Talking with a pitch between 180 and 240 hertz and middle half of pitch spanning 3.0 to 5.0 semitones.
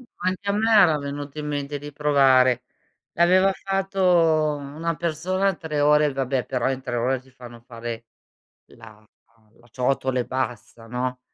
No: medium, 140 Hz; average, 4.7 semitones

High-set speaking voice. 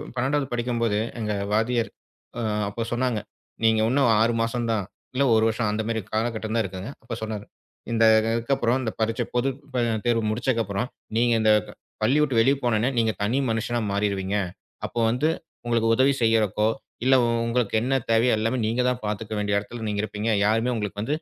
No: low, 115 Hz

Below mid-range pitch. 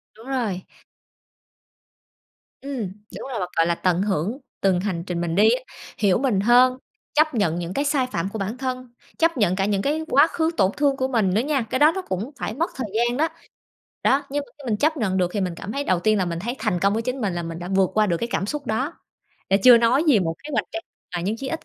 No: high, 220 Hz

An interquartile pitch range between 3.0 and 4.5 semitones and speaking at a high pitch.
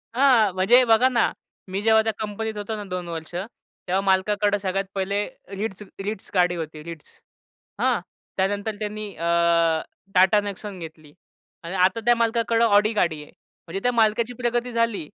Yes: average, 3.3 semitones; high, 205 Hz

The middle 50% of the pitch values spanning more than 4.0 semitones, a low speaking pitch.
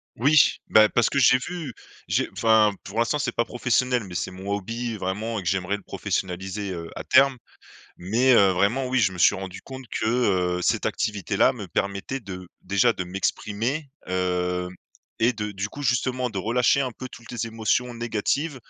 Yes: average, 4.6 semitones; low, 110 Hz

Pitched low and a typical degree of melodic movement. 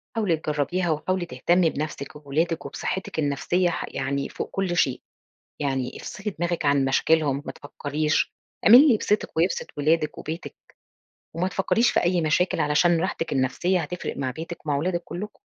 No: medium, 165 Hz; average, 3.6 semitones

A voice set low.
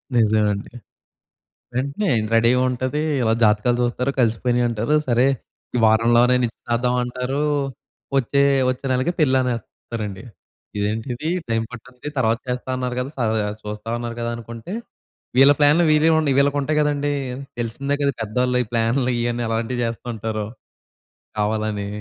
Yes: low, 120 Hz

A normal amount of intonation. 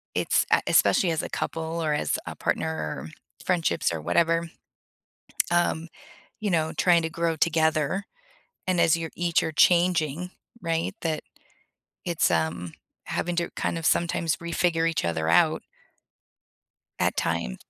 No: narrow, 2.1 semitones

